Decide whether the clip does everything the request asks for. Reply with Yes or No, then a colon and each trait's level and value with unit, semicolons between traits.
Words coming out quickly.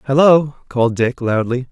No: average, 140 wpm